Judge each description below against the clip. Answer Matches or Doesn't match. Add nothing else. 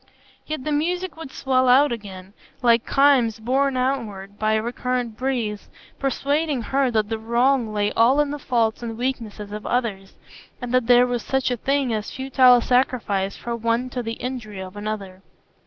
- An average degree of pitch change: Matches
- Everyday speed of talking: Matches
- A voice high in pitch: Matches